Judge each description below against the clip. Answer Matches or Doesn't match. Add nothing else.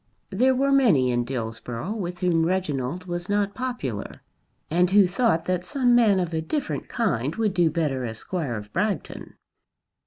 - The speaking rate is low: Doesn't match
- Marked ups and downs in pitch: Matches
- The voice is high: Doesn't match